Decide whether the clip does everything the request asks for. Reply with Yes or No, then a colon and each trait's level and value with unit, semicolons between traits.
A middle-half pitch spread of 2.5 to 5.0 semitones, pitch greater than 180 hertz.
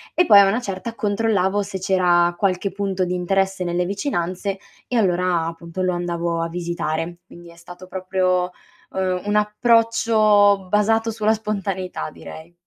Yes: average, 2.8 semitones; high, 190 Hz